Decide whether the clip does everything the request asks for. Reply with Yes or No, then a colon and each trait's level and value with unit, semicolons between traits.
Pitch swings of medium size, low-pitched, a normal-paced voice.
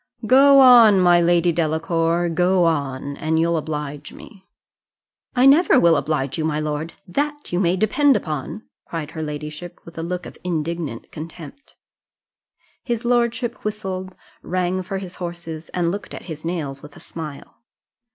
No: average, 3.7 semitones; medium, 170 Hz; average, 155 wpm